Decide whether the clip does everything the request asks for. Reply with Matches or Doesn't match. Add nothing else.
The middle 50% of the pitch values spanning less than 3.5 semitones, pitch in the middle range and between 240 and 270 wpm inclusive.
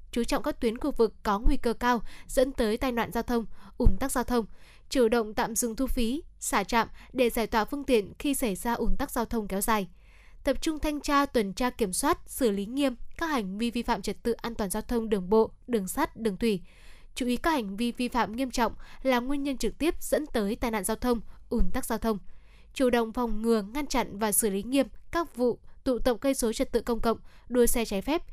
Doesn't match